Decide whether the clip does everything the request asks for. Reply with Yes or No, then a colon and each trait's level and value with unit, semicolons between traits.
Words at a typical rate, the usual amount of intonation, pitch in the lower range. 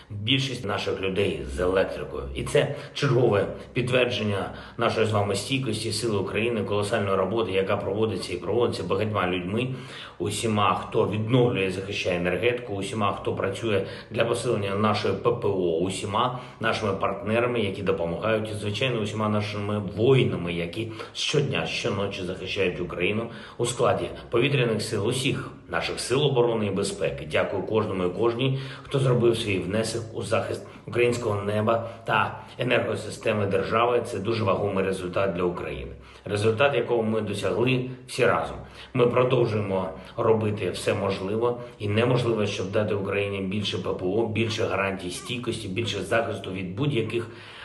Yes: average, 135 wpm; average, 3.2 semitones; low, 105 Hz